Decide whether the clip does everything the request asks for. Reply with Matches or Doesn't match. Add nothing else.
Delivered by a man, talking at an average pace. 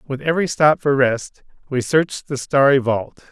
Matches